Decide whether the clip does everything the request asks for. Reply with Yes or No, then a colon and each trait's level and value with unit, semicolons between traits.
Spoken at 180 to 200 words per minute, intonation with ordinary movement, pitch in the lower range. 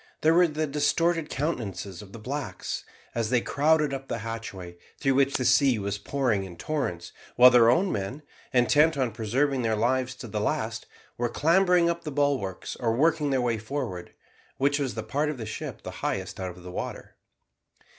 Yes: average, 190 wpm; average, 5.0 semitones; low, 130 Hz